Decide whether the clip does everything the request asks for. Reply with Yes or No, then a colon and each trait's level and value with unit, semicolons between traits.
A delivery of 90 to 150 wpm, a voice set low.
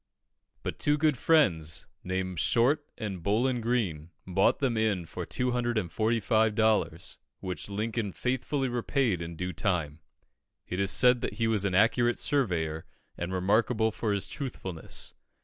Yes: average, 140 wpm; low, 110 Hz